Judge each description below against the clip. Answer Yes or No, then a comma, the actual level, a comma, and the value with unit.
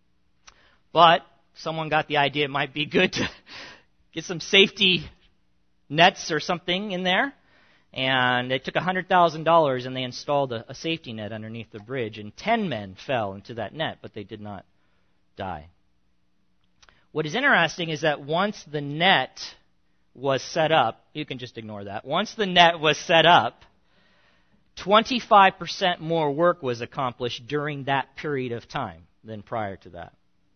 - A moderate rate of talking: Yes, average, 155 wpm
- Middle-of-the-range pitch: Yes, medium, 145 Hz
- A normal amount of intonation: No, wide, 7.0 semitones